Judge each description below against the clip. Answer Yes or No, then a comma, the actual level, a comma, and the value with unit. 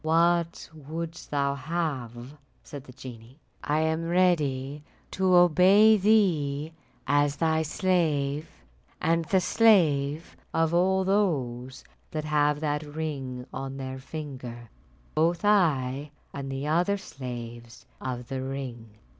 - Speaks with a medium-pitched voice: Yes, medium, 150 Hz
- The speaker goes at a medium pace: No, slow, 120 wpm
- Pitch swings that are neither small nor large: Yes, average, 4.1 semitones